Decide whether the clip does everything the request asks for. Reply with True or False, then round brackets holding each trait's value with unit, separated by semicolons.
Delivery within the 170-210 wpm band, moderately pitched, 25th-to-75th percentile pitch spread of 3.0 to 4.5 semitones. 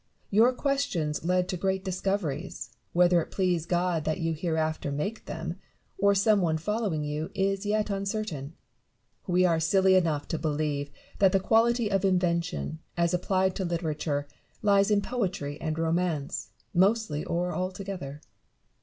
False (145 wpm; 180 Hz; 3.7 semitones)